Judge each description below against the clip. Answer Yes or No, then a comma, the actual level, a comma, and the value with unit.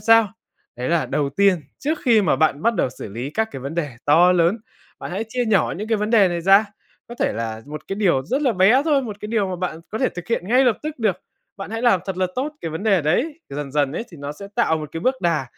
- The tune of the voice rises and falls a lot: Yes, wide, 6.4 semitones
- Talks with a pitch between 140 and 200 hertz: Yes, high, 190 Hz